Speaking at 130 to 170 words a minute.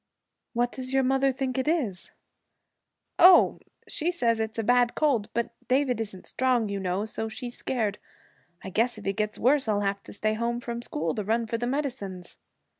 No: average, 190 wpm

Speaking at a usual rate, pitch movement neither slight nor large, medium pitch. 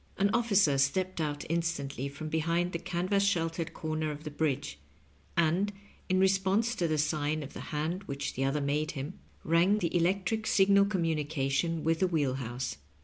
Yes: average, 175 wpm; average, 4.2 semitones; medium, 165 Hz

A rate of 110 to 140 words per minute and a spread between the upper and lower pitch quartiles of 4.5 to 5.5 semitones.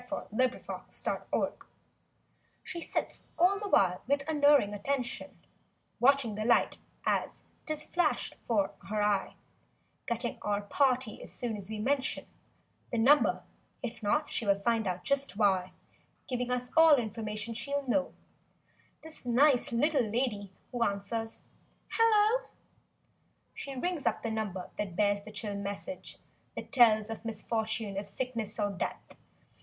Yes: slow, 135 wpm; average, 5.1 semitones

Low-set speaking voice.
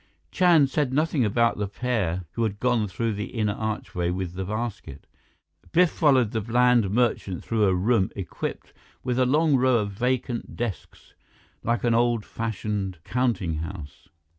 Yes: low, 115 Hz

